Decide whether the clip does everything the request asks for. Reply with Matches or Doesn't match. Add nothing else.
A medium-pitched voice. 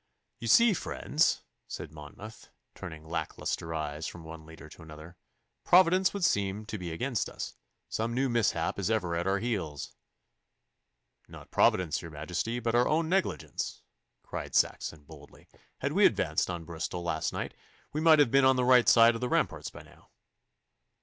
Doesn't match